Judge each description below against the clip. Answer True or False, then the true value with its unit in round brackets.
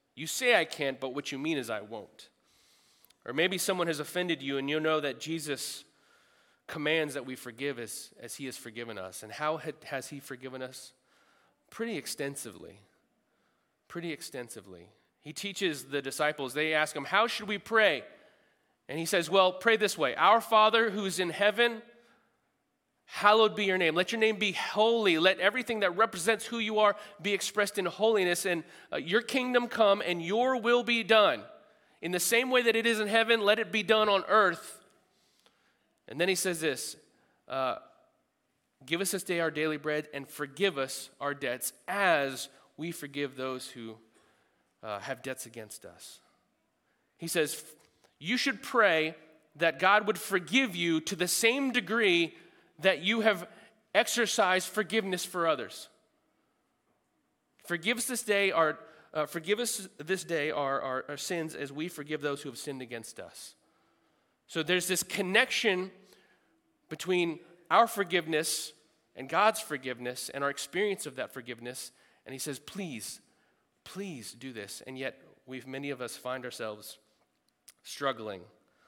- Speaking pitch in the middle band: True (170 Hz)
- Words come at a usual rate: True (165 wpm)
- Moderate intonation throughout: False (6.8 semitones)